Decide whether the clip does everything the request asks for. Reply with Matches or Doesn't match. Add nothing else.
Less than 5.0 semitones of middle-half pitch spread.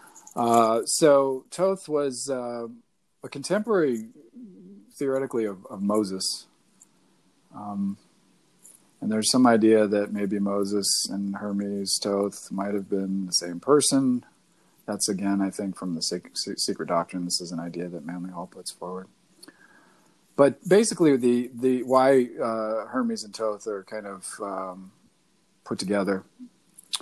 Doesn't match